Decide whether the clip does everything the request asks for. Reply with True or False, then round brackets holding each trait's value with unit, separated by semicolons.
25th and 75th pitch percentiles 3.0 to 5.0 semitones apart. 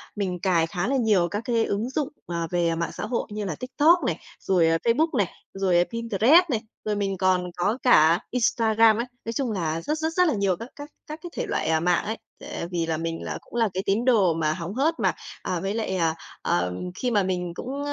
False (5.5 semitones)